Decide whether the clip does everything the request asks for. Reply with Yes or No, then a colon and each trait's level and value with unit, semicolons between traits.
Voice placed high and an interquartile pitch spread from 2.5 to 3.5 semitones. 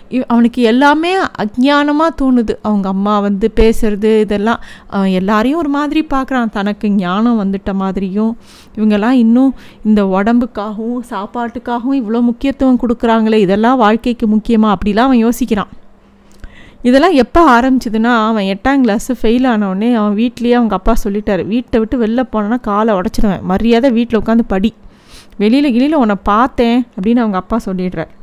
Yes: high, 230 Hz; average, 3.0 semitones